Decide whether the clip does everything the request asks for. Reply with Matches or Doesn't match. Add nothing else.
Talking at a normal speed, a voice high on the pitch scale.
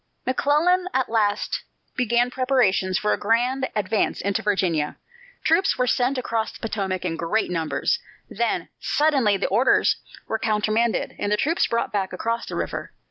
Matches